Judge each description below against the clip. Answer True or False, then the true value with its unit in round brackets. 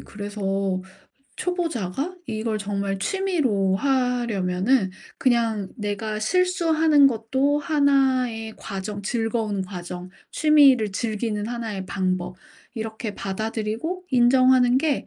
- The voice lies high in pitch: True (225 Hz)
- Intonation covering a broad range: False (4.8 semitones)